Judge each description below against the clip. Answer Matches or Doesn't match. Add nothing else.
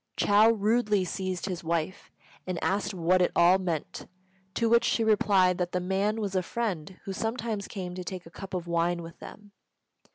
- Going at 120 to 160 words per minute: Doesn't match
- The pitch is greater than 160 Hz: Matches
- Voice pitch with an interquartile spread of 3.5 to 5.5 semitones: Doesn't match